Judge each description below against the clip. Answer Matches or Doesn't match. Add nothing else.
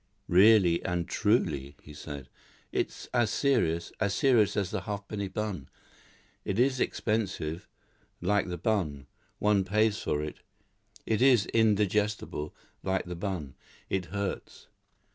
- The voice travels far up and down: Doesn't match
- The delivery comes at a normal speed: Doesn't match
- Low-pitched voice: Matches